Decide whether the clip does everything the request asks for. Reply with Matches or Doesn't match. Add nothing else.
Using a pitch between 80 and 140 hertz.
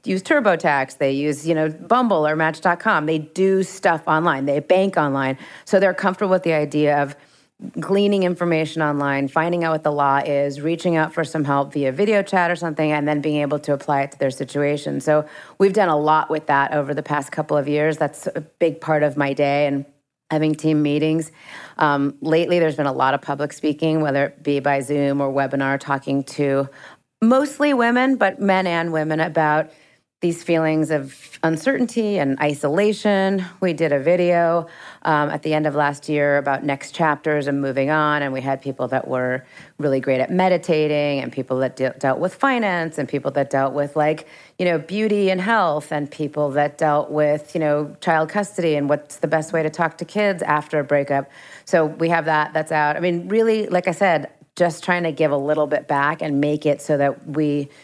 Doesn't match